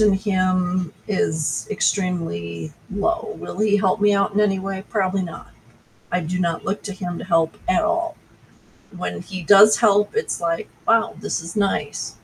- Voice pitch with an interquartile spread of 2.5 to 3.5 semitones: Yes, average, 2.8 semitones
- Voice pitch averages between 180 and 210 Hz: Yes, high, 190 Hz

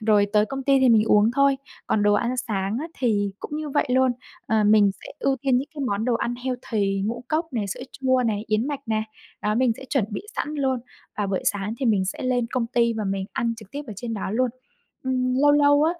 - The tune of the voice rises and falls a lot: No, average, 3.8 semitones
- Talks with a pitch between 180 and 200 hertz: No, high, 235 Hz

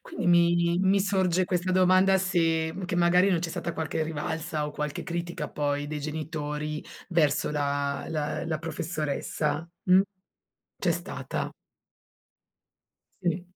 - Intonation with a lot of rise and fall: No, average, 2.8 semitones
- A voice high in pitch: No, medium, 165 Hz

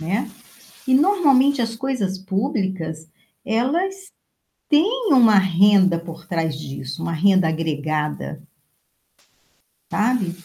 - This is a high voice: Yes, high, 195 Hz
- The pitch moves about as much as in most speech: No, wide, 8.0 semitones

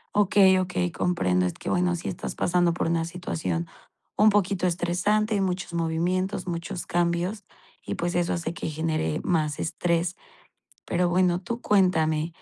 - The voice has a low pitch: No, medium, 175 Hz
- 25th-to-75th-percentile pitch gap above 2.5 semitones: No, narrow, 1.9 semitones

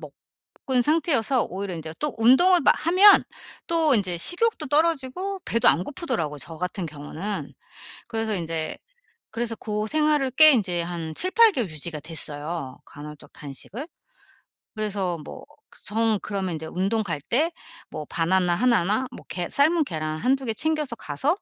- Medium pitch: No, high, 215 Hz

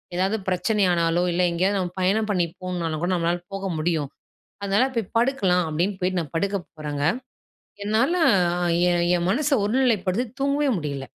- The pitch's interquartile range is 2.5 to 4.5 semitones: Yes, average, 3.6 semitones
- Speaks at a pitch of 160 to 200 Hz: Yes, medium, 185 Hz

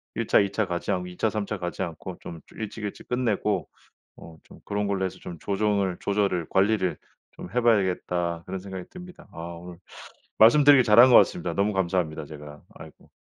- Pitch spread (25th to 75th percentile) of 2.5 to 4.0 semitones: Yes, average, 3.4 semitones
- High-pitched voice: No, low, 100 Hz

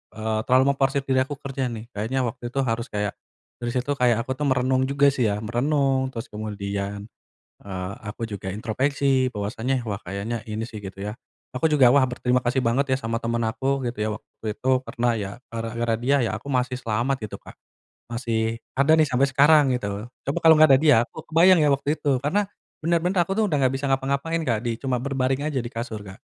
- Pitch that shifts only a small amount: No, average, 3.5 semitones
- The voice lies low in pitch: Yes, low, 125 Hz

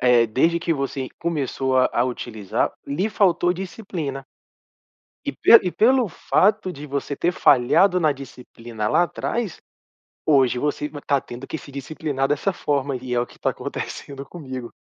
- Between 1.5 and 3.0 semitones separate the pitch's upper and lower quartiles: No, average, 5.2 semitones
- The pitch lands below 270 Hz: Yes, medium, 140 Hz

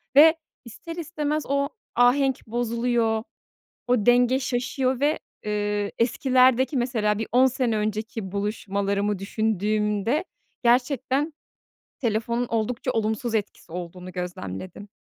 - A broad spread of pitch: No, average, 3.7 semitones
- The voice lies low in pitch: No, high, 235 Hz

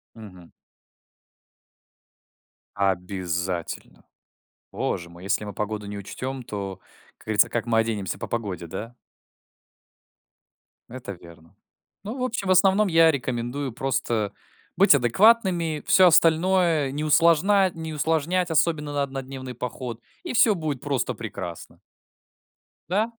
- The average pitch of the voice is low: Yes, low, 130 Hz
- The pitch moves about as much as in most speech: No, wide, 8.2 semitones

